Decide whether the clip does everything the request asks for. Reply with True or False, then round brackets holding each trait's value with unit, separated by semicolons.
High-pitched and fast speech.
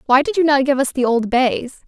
True (270 Hz; 290 wpm)